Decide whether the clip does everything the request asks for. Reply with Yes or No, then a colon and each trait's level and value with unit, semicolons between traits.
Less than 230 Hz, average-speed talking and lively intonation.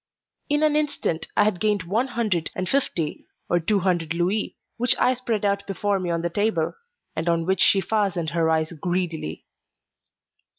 No: medium, 185 Hz; average, 175 wpm; average, 4.3 semitones